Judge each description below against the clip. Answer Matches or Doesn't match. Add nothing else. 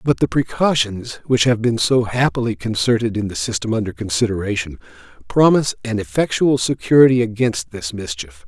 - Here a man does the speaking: Matches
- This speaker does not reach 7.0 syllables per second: Matches